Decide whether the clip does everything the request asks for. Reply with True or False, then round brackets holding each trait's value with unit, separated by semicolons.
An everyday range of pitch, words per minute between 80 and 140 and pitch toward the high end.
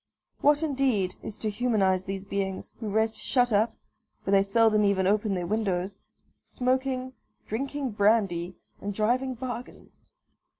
True (4.2 semitones; 135 wpm; 215 Hz)